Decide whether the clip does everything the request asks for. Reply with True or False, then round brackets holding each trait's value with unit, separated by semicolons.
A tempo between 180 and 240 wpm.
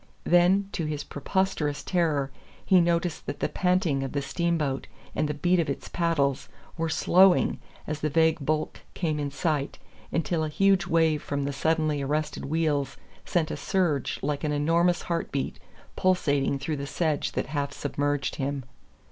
False (165 wpm)